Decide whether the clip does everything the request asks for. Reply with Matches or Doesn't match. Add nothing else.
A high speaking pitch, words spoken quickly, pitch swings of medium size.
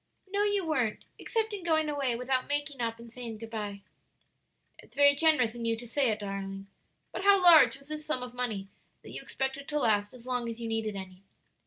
Matches